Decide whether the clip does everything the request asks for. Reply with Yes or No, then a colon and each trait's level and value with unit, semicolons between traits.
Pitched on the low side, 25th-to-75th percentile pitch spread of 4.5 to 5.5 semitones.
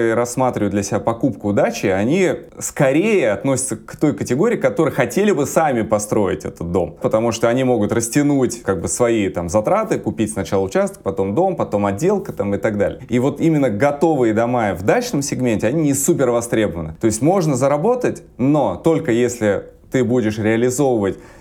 Yes: low, 120 Hz; average, 5.0 semitones